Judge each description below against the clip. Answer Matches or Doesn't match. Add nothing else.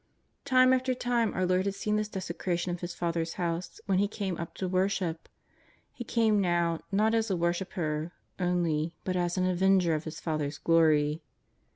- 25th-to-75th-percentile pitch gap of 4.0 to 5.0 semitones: Doesn't match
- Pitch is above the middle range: Doesn't match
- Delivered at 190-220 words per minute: Doesn't match